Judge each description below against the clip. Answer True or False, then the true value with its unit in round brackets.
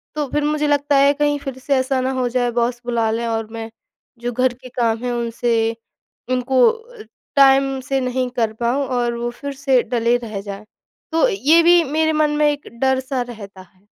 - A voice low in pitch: False (255 Hz)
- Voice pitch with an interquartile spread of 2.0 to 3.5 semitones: True (3.1 semitones)